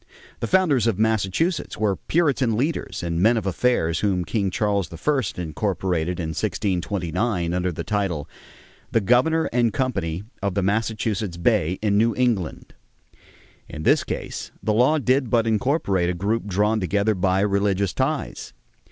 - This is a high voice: No, low, 105 Hz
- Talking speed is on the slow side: No, average, 150 wpm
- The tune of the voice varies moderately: Yes, average, 4.6 semitones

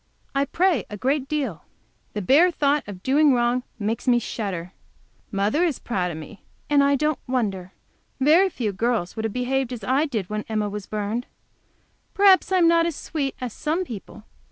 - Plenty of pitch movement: Yes, wide, 6.1 semitones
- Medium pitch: No, very high, 250 Hz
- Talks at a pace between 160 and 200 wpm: Yes, average, 185 wpm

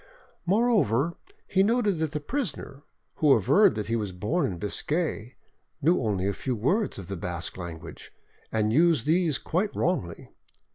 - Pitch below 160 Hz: Yes, medium, 140 Hz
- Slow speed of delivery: No, average, 155 wpm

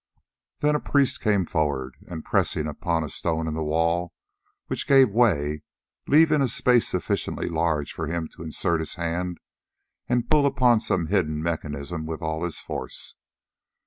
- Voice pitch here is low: Yes, very low, 85 Hz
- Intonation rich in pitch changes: Yes, wide, 6.7 semitones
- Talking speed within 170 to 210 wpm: No, average, 160 wpm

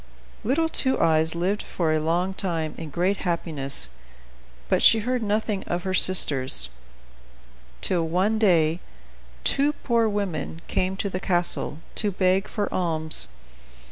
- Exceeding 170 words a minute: No, average, 140 wpm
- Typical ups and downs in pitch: Yes, average, 4.2 semitones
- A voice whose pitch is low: No, medium, 180 Hz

